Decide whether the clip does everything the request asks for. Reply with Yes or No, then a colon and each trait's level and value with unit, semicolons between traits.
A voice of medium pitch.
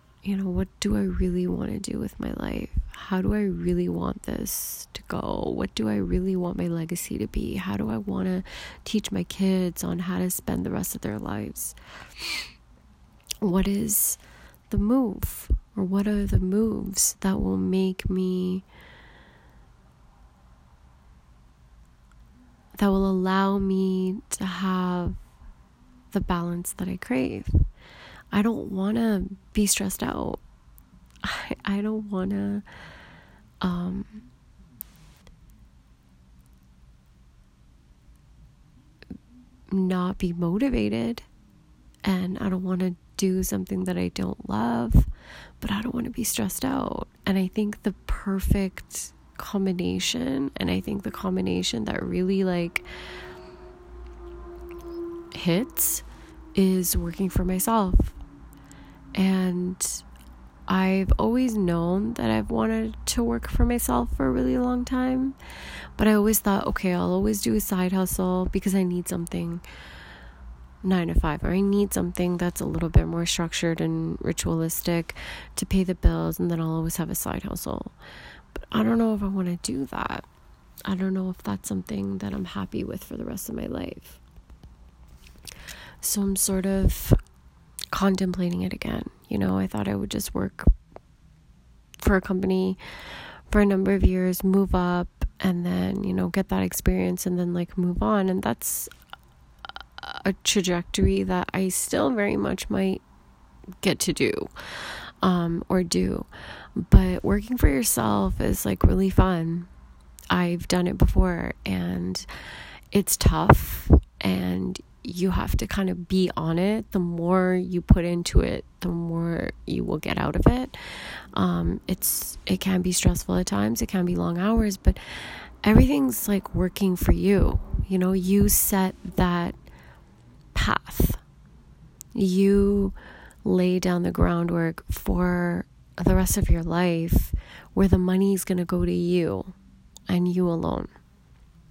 Yes: medium, 175 Hz